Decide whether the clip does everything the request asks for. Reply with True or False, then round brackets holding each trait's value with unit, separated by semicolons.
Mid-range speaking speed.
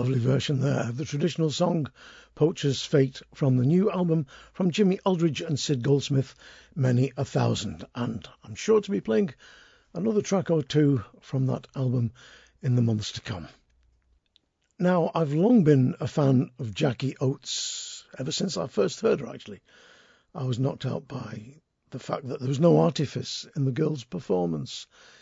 True (170 wpm)